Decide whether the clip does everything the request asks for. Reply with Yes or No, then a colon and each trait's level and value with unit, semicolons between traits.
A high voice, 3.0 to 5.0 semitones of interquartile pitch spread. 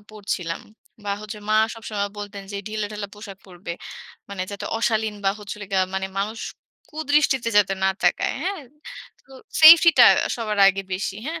No: high, 210 Hz; narrow, 2.4 semitones